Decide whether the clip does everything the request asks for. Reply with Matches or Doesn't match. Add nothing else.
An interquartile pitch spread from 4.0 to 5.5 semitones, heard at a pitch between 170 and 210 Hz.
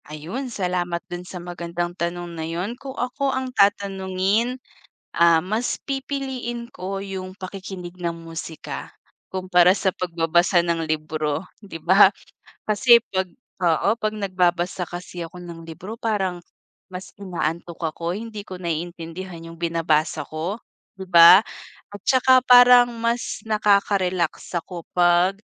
Doesn't match